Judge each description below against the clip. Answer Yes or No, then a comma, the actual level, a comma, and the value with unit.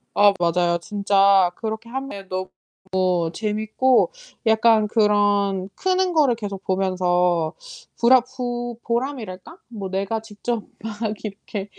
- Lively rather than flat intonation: No, average, 3.8 semitones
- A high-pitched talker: Yes, high, 205 Hz